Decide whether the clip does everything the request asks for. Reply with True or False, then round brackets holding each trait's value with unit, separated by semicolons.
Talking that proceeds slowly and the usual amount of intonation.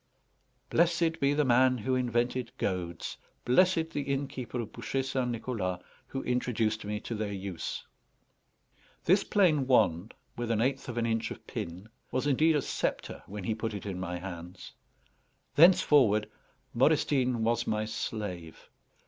False (150 wpm; 4.3 semitones)